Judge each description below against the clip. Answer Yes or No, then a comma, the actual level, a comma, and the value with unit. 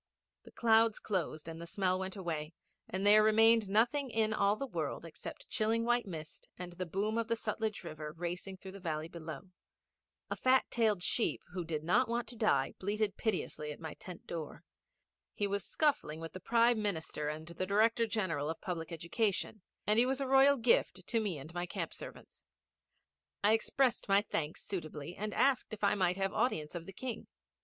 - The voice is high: Yes, high, 200 Hz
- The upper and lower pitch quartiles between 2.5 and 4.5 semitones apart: No, average, 4.9 semitones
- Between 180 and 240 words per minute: Yes, average, 195 wpm